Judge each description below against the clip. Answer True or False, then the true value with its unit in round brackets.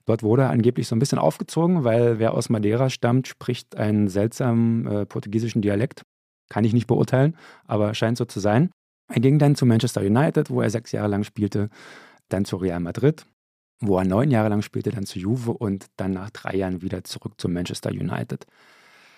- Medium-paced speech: False (195 wpm)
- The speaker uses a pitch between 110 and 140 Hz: True (115 Hz)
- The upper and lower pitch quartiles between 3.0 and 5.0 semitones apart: True (3.9 semitones)